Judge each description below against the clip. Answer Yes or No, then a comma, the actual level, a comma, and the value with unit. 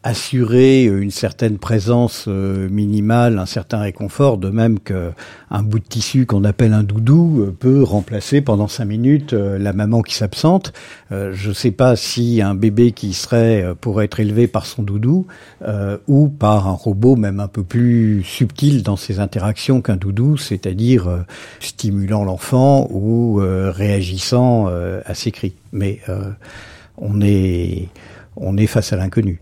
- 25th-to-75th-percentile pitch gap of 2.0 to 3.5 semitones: Yes, average, 3.2 semitones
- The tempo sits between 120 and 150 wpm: Yes, slow, 145 wpm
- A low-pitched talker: Yes, low, 105 Hz